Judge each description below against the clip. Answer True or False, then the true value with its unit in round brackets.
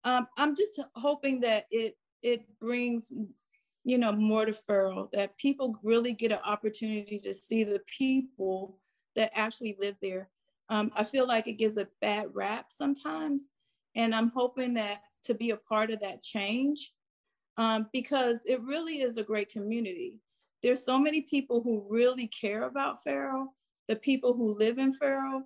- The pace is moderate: True (165 wpm)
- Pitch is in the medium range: False (230 Hz)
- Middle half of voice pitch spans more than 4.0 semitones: False (3.7 semitones)